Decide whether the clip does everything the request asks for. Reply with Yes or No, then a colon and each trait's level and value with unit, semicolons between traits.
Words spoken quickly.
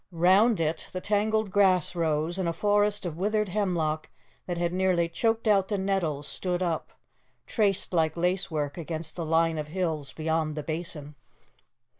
No: average, 160 wpm